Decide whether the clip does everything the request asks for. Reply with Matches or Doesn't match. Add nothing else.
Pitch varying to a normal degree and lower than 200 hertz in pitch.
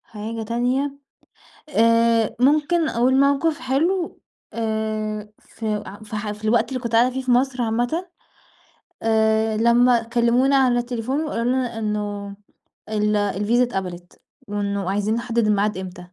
Doesn't match